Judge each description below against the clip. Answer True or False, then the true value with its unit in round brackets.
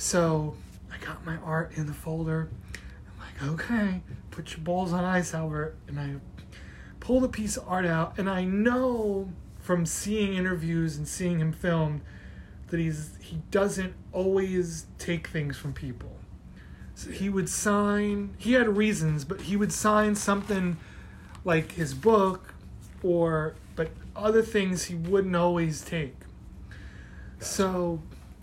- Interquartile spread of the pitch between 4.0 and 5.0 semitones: True (4.3 semitones)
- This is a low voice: False (175 Hz)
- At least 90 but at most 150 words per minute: True (145 wpm)